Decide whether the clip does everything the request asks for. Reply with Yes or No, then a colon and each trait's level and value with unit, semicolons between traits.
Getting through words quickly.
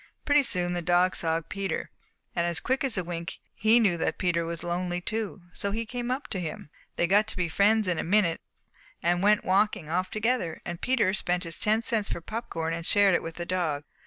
Yes: fast, 220 wpm